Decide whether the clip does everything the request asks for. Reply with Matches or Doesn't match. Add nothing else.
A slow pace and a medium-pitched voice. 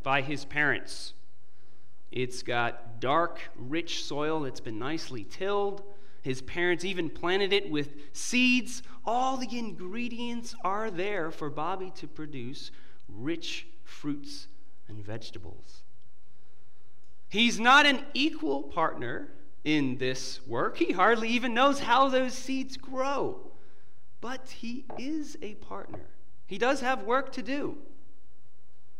Matches